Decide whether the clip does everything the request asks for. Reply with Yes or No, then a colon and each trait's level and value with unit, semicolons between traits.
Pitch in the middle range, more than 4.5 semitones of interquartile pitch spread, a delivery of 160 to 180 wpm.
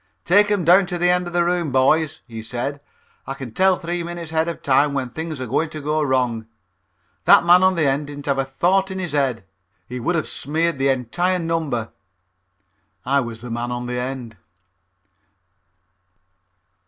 No: medium, 145 Hz; average, 5.1 semitones; average, 190 wpm